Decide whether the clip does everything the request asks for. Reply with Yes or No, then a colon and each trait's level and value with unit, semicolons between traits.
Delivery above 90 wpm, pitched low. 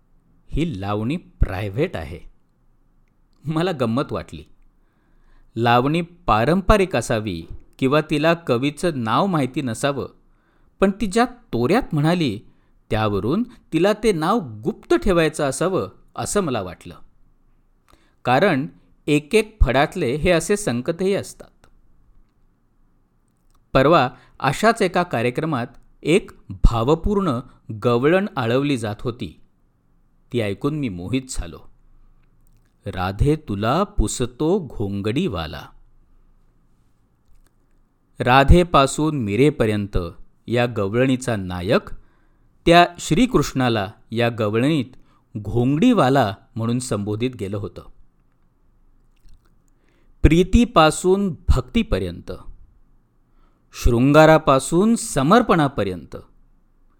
No: slow, 80 wpm; low, 130 Hz